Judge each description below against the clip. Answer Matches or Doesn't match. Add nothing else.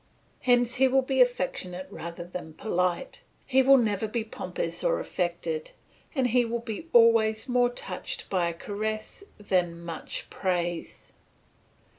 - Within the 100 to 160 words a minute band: Matches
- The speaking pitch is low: Doesn't match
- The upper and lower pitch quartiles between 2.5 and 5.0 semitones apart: Doesn't match